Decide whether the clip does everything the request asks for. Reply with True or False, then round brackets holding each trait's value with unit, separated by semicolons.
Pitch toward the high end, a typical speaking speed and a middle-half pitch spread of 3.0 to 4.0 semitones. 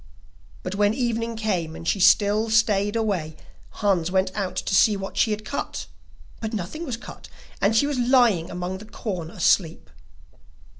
True (205 Hz; 165 wpm; 3.4 semitones)